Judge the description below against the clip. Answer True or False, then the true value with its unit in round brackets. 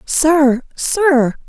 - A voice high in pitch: True (290 Hz)